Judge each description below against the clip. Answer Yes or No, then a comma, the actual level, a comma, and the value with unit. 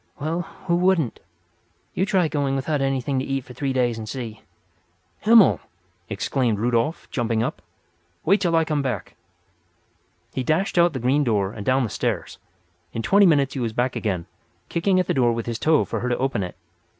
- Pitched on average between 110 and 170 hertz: Yes, low, 135 Hz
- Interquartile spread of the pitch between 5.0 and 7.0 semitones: Yes, wide, 5.4 semitones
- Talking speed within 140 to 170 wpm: No, average, 190 wpm